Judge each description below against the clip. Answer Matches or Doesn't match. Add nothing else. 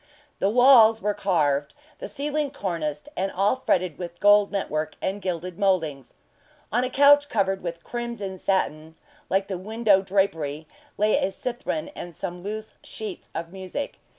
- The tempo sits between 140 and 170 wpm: Matches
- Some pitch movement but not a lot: Matches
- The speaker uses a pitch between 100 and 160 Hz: Doesn't match